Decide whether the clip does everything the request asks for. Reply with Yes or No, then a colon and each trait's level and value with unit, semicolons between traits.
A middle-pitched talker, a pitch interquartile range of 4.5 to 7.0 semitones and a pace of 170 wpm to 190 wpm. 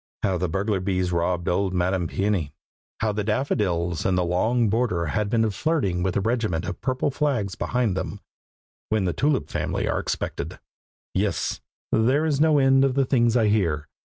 No: low, 105 Hz; wide, 5.6 semitones; average, 180 wpm